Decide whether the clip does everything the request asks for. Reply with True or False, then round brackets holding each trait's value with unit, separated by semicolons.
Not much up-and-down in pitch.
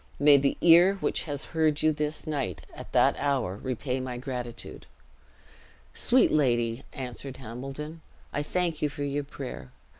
False (3.2 semitones)